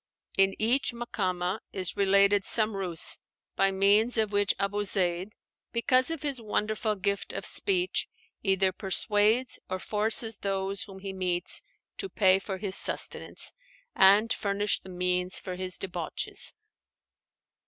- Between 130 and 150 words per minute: Yes, slow, 135 wpm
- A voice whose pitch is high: Yes, high, 200 Hz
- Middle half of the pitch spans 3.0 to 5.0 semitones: No, narrow, 2.4 semitones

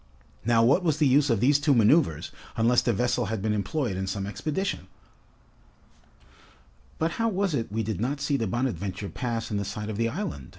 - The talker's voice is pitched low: Yes, low, 120 Hz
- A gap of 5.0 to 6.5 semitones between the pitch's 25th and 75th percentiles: Yes, wide, 5.5 semitones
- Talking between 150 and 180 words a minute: No, average, 200 wpm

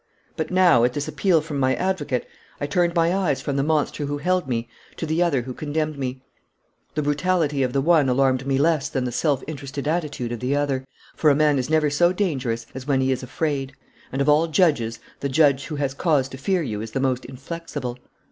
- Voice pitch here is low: No, medium, 145 Hz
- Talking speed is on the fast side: Yes, fast, 225 wpm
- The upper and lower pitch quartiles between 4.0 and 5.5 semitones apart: No, average, 3.2 semitones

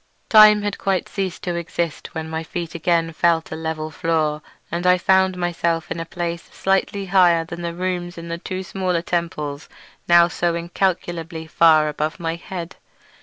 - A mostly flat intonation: Yes, narrow, 1.8 semitones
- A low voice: No, medium, 170 Hz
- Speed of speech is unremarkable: Yes, average, 170 wpm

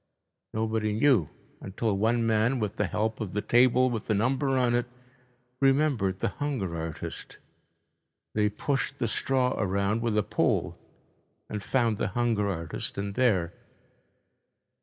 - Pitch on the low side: Yes, low, 110 Hz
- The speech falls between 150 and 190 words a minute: No, average, 140 wpm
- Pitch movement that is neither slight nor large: Yes, average, 3.8 semitones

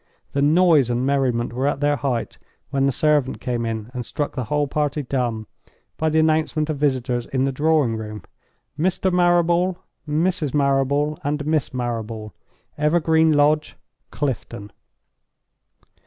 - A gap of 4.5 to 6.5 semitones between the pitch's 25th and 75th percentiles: No, average, 3.8 semitones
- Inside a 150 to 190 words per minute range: No, average, 140 wpm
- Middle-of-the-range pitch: Yes, medium, 145 Hz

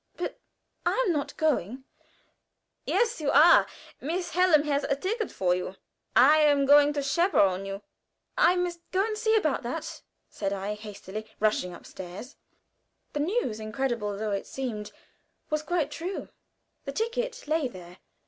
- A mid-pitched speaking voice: No, very high, 285 Hz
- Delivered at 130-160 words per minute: Yes, average, 150 wpm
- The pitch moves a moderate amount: No, wide, 8.7 semitones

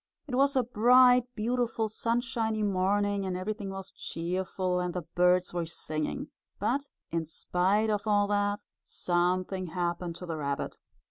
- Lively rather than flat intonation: No, average, 3.7 semitones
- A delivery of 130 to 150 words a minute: Yes, average, 145 wpm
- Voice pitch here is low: No, high, 195 Hz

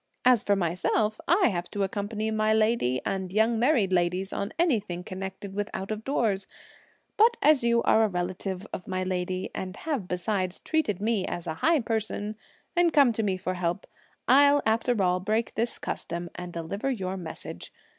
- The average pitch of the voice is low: No, high, 205 Hz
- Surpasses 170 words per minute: Yes, average, 180 wpm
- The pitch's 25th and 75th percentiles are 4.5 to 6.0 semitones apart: No, average, 4.0 semitones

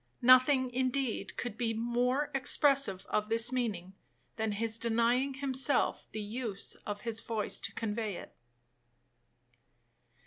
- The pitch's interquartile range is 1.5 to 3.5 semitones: Yes, average, 2.9 semitones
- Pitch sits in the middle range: No, high, 235 Hz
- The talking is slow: Yes, slow, 125 wpm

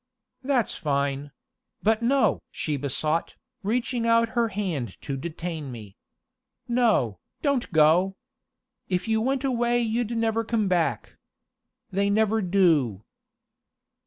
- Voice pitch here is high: Yes, high, 200 Hz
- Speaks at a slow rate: Yes, slow, 115 wpm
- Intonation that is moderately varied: No, wide, 7.3 semitones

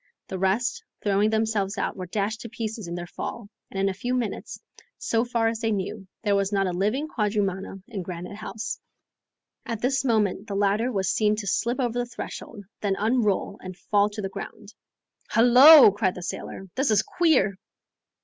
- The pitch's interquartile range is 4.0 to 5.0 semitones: No, average, 3.0 semitones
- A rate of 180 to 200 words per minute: Yes, average, 190 wpm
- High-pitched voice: Yes, high, 210 Hz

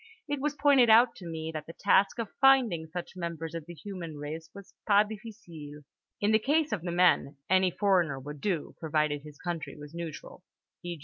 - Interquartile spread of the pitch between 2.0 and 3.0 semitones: No, average, 5.0 semitones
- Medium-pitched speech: Yes, medium, 175 Hz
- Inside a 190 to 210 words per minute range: Yes, average, 195 wpm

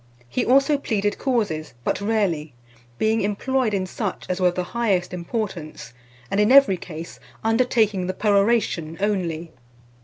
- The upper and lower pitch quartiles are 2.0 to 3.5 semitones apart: No, average, 4.2 semitones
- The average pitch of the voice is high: Yes, high, 200 Hz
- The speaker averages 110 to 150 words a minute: Yes, average, 145 wpm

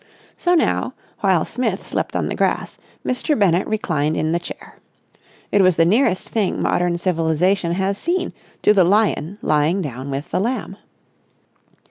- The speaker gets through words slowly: No, average, 155 wpm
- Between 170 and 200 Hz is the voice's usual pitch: Yes, medium, 185 Hz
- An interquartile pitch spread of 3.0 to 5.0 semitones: Yes, average, 4.1 semitones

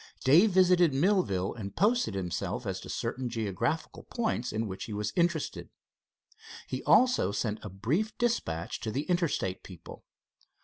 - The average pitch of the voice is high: No, low, 125 Hz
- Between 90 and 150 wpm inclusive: Yes, average, 145 wpm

